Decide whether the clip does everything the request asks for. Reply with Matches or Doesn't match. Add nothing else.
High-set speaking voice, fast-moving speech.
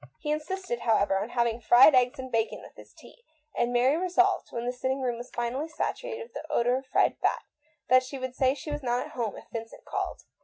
Matches